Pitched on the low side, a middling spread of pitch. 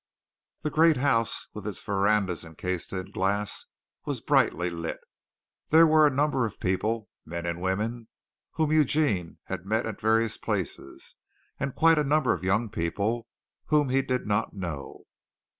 No: low, 110 Hz; wide, 6.7 semitones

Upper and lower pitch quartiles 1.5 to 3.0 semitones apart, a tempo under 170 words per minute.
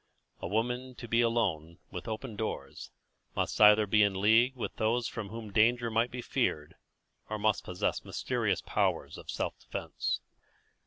Yes: narrow, 2.4 semitones; average, 160 wpm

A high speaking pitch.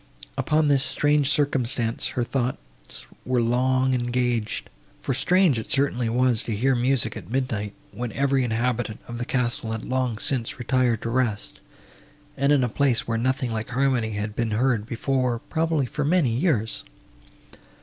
No: low, 125 Hz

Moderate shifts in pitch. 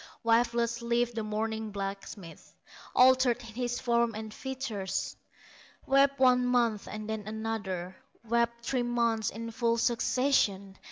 No: narrow, 2.1 semitones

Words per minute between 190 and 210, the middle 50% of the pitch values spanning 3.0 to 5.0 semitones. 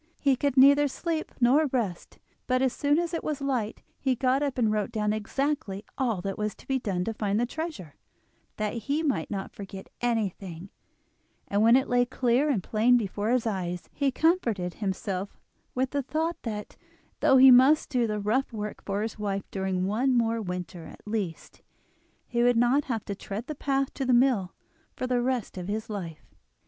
Yes: average, 195 wpm; average, 4.7 semitones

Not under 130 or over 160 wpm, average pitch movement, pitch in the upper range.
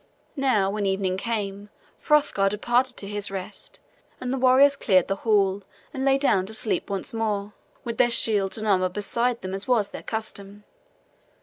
No: average, 175 wpm; average, 3.3 semitones; high, 210 Hz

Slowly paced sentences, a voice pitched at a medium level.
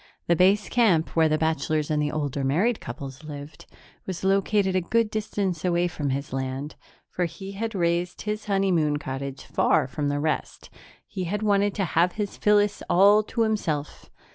No: average, 175 wpm; medium, 175 Hz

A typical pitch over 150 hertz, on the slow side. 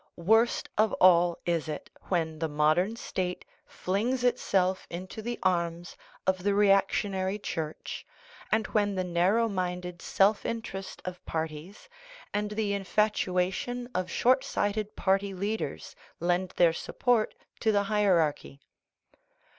Yes: high, 190 Hz; slow, 125 wpm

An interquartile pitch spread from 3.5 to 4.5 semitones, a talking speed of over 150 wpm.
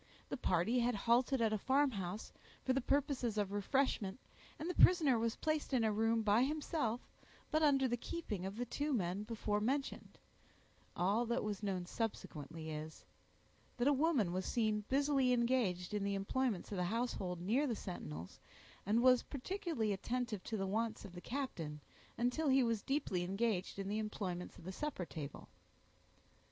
No: average, 5.2 semitones; average, 170 wpm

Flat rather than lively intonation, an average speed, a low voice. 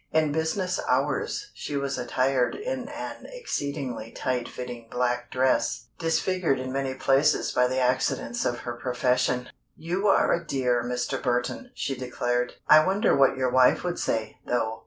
No: average, 4.1 semitones; average, 155 wpm; low, 130 Hz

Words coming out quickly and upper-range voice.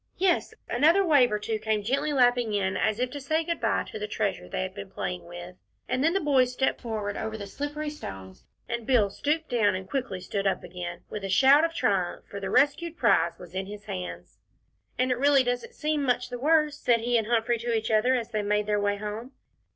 Yes: fast, 230 wpm; high, 230 Hz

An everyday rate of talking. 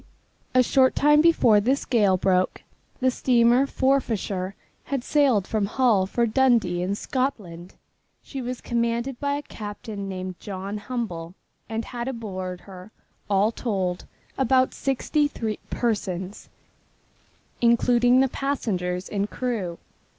No: slow, 120 wpm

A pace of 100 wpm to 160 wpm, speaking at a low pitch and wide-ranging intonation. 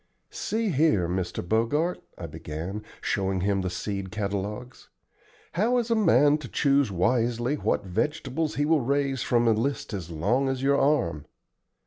Yes: average, 155 wpm; low, 120 Hz; wide, 6.8 semitones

